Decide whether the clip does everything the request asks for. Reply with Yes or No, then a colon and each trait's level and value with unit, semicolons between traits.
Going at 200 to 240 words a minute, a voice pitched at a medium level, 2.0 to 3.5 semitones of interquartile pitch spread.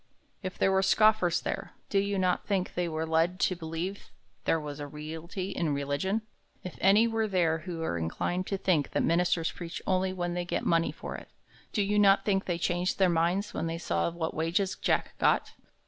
Yes: fast, 205 wpm; medium, 180 Hz; average, 2.8 semitones